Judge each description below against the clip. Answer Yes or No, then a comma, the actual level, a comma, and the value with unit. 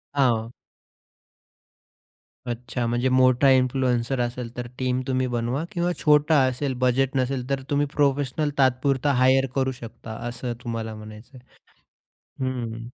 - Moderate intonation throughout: No, narrow, 2.1 semitones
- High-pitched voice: No, low, 130 Hz